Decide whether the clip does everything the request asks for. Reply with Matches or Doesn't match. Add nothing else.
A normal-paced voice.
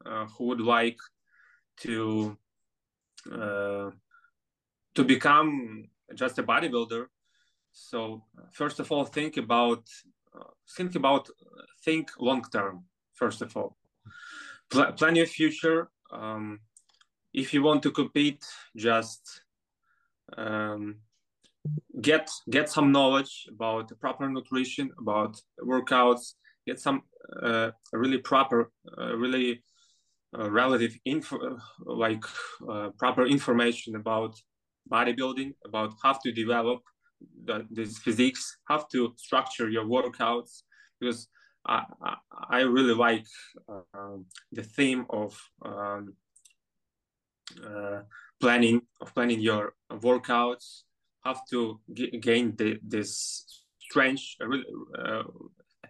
Doesn't match